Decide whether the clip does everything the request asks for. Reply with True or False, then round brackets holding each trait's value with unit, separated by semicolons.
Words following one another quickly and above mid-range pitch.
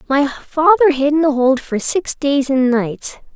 False (195 wpm; 285 Hz)